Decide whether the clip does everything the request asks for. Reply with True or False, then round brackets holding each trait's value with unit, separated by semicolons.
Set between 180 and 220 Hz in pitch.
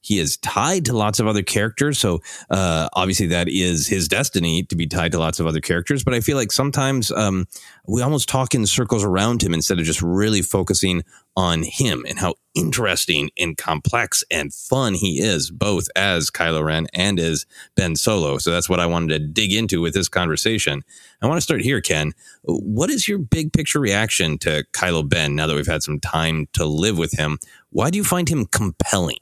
False (95 Hz)